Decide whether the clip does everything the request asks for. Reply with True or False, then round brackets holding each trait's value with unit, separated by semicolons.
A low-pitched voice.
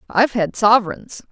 False (215 Hz)